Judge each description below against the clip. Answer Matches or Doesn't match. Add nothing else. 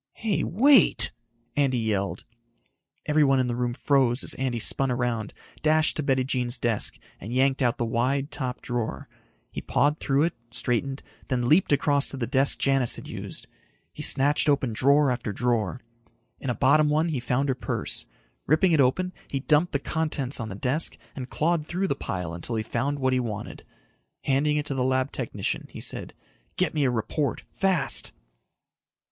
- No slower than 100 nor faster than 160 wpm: Doesn't match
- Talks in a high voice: Doesn't match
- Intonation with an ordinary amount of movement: Matches